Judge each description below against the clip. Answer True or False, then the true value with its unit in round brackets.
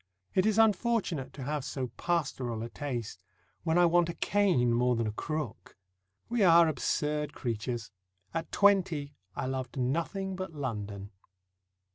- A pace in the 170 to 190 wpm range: False (145 wpm)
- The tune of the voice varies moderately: False (6.0 semitones)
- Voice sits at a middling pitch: True (150 Hz)